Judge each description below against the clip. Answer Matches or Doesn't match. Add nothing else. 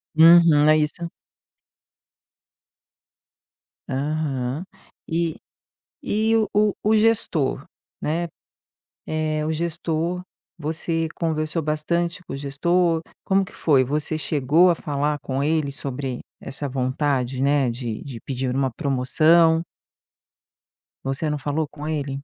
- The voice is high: Doesn't match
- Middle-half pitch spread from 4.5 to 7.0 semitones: Doesn't match